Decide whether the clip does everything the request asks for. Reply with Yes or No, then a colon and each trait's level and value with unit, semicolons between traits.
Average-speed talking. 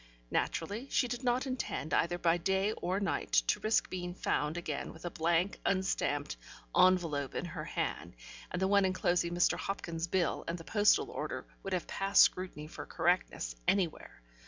Yes: average, 170 wpm